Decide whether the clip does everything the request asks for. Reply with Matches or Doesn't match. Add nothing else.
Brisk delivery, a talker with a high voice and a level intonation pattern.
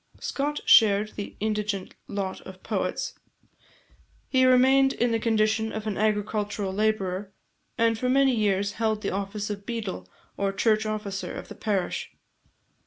Doesn't match